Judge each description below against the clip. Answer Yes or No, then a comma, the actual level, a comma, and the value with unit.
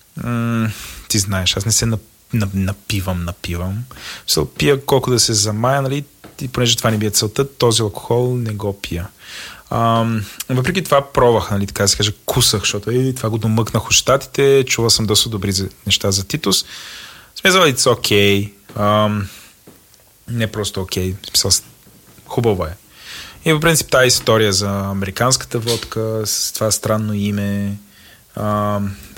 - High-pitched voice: No, low, 110 Hz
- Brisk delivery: No, average, 155 wpm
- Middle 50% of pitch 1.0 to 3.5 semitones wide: Yes, average, 3.0 semitones